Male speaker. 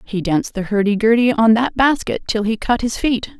No: female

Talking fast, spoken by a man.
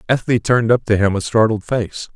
Yes: fast, 220 wpm; male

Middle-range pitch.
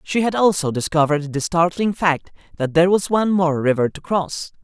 Yes: medium, 170 Hz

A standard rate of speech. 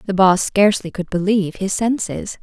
Yes: average, 175 wpm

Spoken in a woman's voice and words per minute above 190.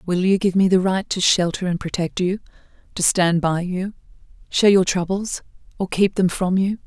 Yes: female; average, 200 wpm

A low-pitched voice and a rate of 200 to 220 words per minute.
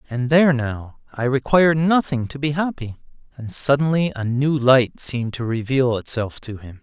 No: low, 130 Hz; average, 175 wpm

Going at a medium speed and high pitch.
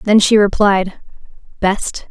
No: slow, 115 wpm; high, 200 Hz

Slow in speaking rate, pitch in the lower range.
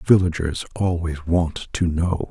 Yes: slow, 130 wpm; very low, 85 Hz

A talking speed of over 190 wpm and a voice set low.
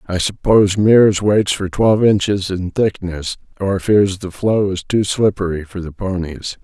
No: average, 170 wpm; very low, 95 Hz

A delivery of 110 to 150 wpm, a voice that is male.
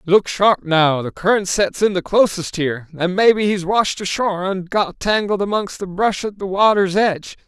No: average, 200 wpm; male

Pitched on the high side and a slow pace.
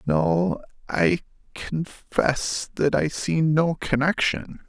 No: medium, 140 Hz; slow, 105 wpm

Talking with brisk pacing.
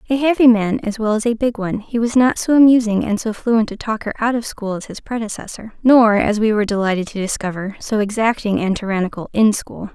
Yes: fast, 230 wpm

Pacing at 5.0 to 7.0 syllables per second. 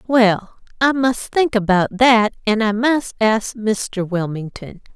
No: 3.5 syllables/s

